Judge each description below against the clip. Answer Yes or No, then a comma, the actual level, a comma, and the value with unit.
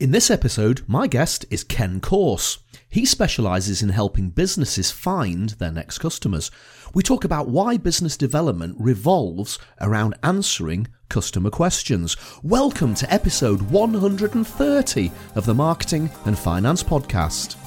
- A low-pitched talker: Yes, low, 130 Hz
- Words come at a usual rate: No, slow, 130 wpm